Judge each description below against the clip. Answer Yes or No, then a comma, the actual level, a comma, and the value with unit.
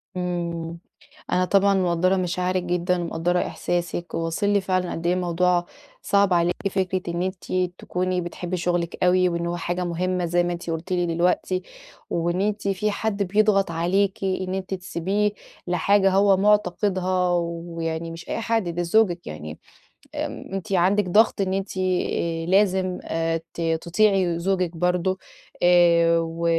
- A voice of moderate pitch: Yes, medium, 180 Hz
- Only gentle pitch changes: Yes, narrow, 1.8 semitones